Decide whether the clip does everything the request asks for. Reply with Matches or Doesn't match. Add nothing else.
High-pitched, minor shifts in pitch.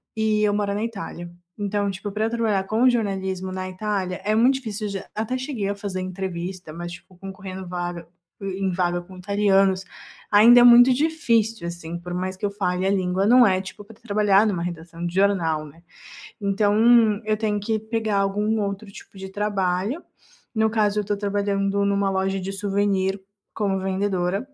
Matches